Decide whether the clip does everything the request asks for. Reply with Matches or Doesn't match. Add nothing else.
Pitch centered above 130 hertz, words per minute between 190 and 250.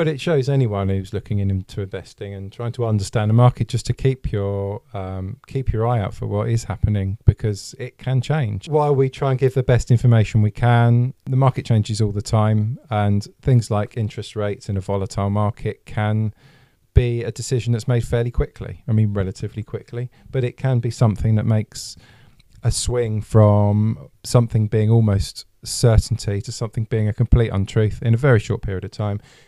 Doesn't match